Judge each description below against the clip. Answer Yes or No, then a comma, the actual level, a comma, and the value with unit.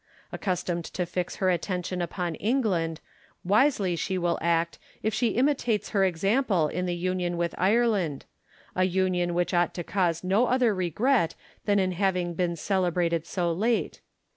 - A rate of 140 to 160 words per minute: Yes, average, 155 wpm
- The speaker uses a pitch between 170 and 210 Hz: Yes, medium, 185 Hz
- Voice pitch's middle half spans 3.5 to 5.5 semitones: No, average, 2.9 semitones